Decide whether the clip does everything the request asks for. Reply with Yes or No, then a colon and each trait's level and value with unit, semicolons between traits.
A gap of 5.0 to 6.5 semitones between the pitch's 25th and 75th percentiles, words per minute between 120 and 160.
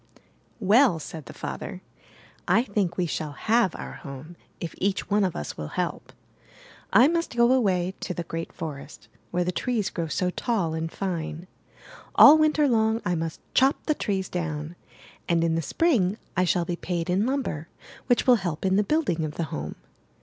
No: wide, 5.5 semitones; average, 185 wpm